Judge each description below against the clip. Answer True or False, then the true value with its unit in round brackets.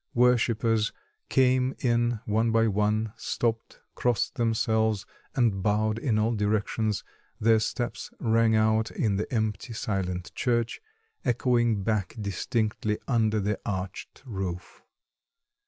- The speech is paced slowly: True (115 wpm)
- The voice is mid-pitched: False (110 Hz)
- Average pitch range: False (2.0 semitones)